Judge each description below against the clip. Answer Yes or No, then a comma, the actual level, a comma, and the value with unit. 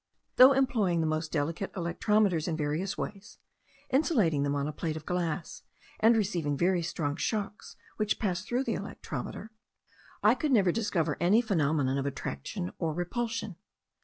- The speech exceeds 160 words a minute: No, average, 155 wpm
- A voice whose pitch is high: No, medium, 175 Hz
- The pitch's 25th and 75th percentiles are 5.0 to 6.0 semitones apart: Yes, wide, 5.4 semitones